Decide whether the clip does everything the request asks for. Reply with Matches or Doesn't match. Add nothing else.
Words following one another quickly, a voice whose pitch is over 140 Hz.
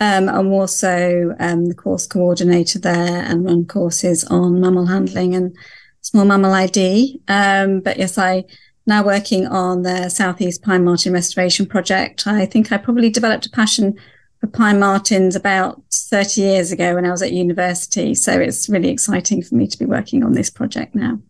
Doesn't match